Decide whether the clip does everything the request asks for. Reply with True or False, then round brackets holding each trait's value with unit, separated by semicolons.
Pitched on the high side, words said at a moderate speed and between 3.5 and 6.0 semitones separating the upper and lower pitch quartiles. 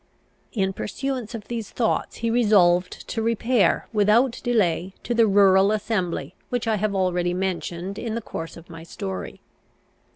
True (205 Hz; 155 wpm; 4.1 semitones)